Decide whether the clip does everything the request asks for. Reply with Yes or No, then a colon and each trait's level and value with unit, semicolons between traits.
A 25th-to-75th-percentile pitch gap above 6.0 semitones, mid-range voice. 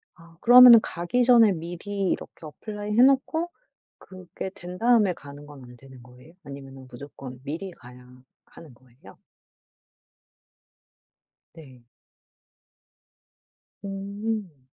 Yes: wide, 7.5 semitones; medium, 170 Hz